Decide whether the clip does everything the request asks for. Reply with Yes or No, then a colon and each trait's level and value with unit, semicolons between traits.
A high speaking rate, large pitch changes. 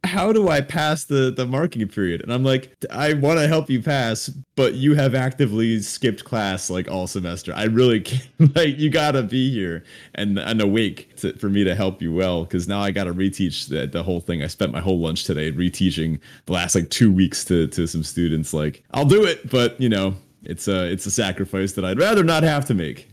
Yes: fast, 230 wpm; wide, 6.5 semitones